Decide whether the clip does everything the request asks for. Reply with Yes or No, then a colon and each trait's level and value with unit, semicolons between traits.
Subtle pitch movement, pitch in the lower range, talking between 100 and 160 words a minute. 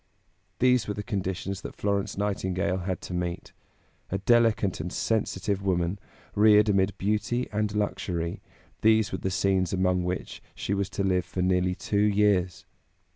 Yes: narrow, 2.2 semitones; very low, 95 Hz; average, 155 wpm